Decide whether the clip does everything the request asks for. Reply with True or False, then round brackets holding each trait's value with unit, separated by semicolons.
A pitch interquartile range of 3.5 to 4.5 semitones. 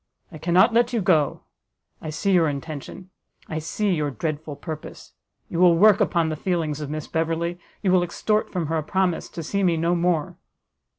False (3.0 semitones)